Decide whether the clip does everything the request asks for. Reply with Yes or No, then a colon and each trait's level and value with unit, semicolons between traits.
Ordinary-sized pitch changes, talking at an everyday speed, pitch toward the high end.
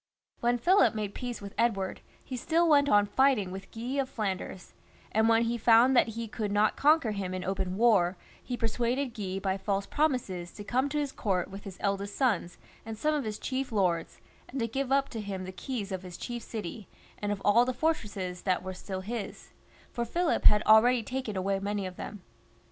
No: average, 4.3 semitones; fast, 210 wpm; high, 215 Hz